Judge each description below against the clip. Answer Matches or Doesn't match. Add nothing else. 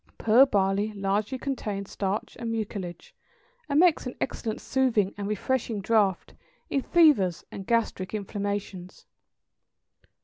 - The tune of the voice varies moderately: Matches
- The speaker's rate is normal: Doesn't match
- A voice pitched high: Matches